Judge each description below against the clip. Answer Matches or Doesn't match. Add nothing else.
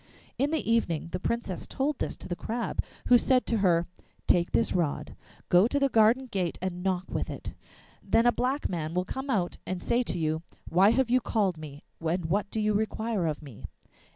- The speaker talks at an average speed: Doesn't match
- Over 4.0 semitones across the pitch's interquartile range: Matches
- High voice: Matches